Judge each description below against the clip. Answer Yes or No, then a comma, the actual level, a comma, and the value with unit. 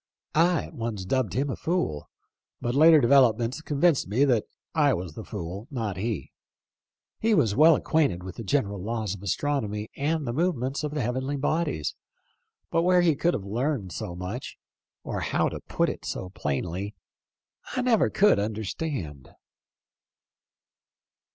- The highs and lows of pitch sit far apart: Yes, wide, 7.0 semitones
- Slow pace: No, average, 155 wpm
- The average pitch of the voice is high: No, low, 125 Hz